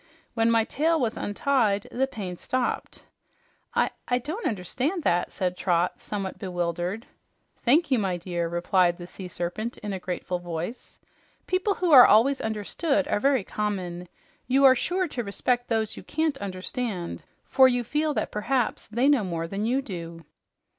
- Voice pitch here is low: No, high, 220 Hz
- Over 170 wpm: No, average, 165 wpm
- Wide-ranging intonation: Yes, wide, 6.5 semitones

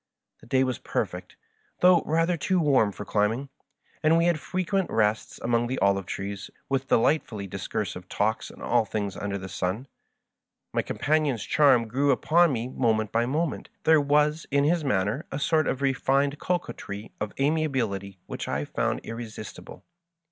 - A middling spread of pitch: No, wide, 6.3 semitones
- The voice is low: Yes, low, 130 Hz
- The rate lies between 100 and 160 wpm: No, average, 170 wpm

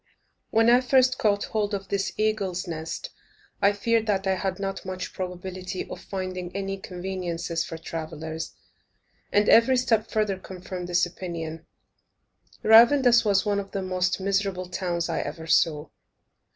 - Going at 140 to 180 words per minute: Yes, average, 150 wpm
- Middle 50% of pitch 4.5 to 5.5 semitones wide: No, average, 2.8 semitones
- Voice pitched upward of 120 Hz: Yes, high, 190 Hz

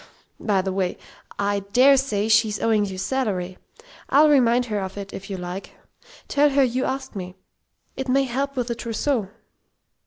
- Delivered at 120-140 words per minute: No, average, 175 wpm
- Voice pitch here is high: Yes, high, 225 Hz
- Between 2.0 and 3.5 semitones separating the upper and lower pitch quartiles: No, average, 5.2 semitones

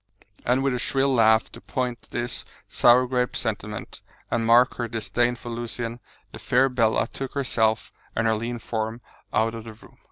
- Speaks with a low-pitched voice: Yes, low, 120 Hz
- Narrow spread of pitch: Yes, narrow, 1.9 semitones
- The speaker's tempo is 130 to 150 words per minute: No, average, 180 wpm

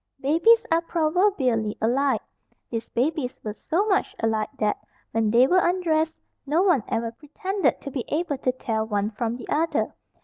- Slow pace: No, average, 165 wpm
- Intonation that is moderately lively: No, wide, 6.8 semitones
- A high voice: Yes, very high, 275 Hz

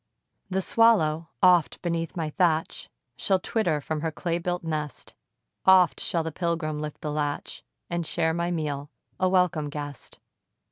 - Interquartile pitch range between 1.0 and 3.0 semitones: Yes, narrow, 2.6 semitones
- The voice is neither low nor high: Yes, medium, 165 Hz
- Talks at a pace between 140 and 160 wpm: Yes, average, 150 wpm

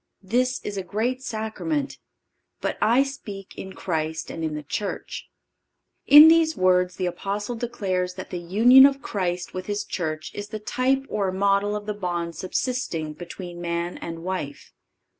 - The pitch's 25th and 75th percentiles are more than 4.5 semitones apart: Yes, average, 5.2 semitones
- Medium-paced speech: Yes, average, 160 wpm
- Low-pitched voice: No, high, 195 Hz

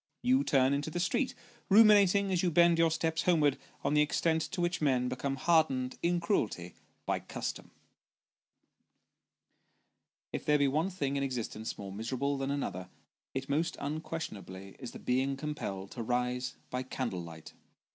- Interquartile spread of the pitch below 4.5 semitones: No, average, 4.9 semitones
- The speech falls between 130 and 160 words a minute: Yes, average, 155 wpm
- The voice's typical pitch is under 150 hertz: Yes, medium, 140 Hz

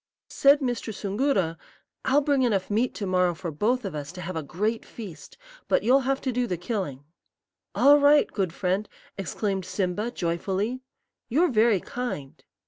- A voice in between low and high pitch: No, high, 210 Hz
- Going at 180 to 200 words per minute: No, average, 165 wpm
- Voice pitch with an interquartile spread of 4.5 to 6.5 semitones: Yes, wide, 5.6 semitones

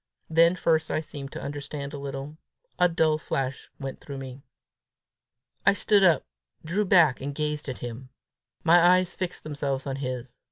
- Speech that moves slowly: No, average, 165 wpm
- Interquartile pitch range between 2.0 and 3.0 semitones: No, average, 3.6 semitones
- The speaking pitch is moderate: Yes, medium, 145 Hz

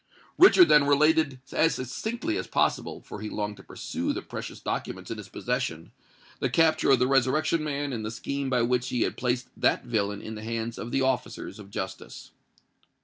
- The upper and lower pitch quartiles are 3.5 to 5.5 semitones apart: Yes, average, 4.4 semitones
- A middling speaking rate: Yes, average, 185 wpm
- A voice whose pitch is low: Yes, low, 125 Hz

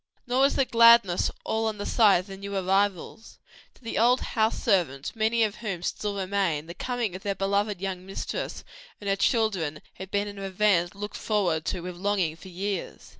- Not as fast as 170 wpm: No, average, 195 wpm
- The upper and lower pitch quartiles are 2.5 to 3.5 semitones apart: Yes, average, 3.0 semitones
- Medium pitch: No, high, 200 Hz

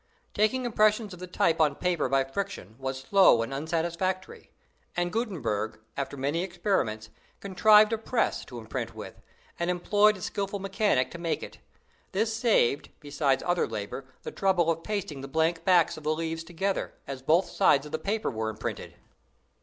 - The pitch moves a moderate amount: No, wide, 6.3 semitones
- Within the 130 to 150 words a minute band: No, average, 170 wpm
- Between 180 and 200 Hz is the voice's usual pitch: No, medium, 170 Hz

